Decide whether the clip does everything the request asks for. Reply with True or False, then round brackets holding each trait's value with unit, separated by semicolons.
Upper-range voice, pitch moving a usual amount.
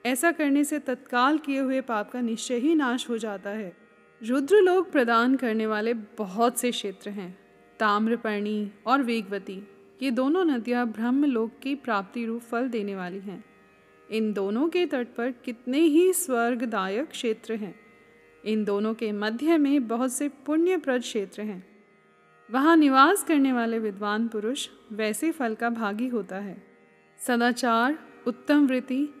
True (235 Hz; 4.1 semitones)